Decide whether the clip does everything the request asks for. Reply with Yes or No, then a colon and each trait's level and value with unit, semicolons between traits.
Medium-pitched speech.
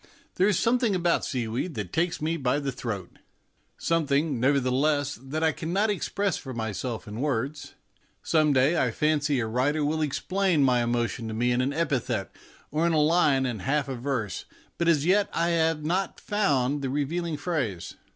Yes: medium, 145 Hz